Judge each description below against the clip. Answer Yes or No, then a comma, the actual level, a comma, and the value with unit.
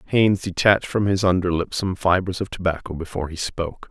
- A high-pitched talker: No, very low, 90 Hz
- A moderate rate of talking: Yes, average, 185 wpm